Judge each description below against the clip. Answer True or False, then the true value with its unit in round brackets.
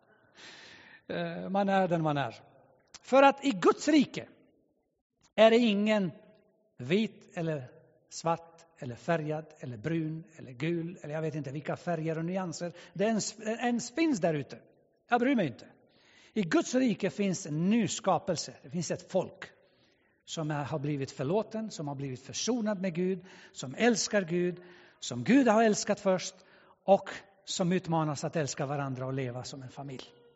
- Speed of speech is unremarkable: True (155 wpm)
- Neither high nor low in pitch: True (175 Hz)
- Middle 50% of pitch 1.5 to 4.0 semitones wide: False (5.4 semitones)